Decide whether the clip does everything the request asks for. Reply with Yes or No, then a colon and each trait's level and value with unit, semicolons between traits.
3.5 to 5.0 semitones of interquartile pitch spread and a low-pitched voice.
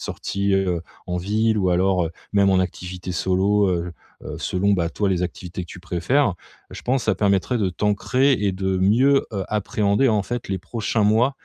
No: average, 2.8 semitones; low, 100 Hz